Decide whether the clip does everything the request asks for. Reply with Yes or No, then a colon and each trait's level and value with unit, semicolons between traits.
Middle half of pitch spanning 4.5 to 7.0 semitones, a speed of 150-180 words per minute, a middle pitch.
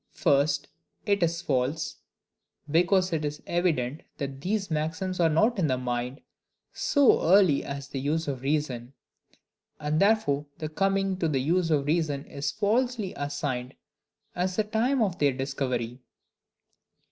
No: average, 5.1 semitones; average, 140 wpm; medium, 155 Hz